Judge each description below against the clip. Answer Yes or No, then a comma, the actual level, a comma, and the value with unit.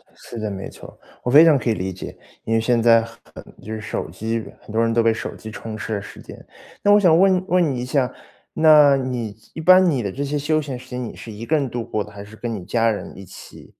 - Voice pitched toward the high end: No, low, 115 Hz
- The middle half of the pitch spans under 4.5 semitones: No, average, 4.9 semitones